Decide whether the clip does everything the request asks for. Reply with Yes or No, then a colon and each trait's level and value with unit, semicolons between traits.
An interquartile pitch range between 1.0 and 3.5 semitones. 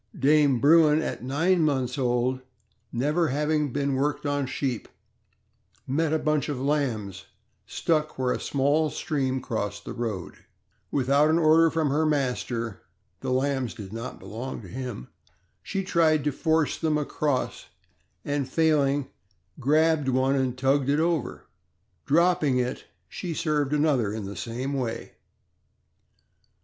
Yes: average, 3.2 semitones